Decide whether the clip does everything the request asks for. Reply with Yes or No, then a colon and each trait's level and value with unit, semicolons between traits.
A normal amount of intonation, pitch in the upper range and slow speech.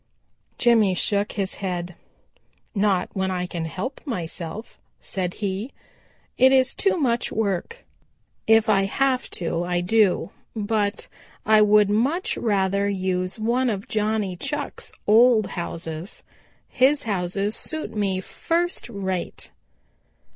Yes: average, 3.7 semitones; high, 205 Hz; slow, 120 wpm